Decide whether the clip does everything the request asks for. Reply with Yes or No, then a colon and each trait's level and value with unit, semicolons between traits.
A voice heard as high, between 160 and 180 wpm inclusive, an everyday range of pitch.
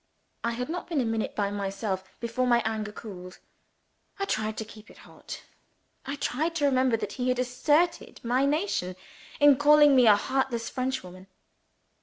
Yes: high, 245 Hz; average, 170 wpm; average, 4.6 semitones